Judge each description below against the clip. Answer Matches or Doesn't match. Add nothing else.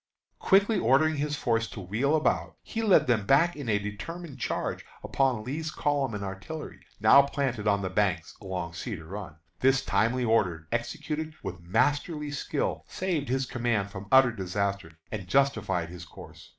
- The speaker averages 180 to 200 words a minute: Doesn't match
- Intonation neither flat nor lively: Doesn't match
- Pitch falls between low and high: Doesn't match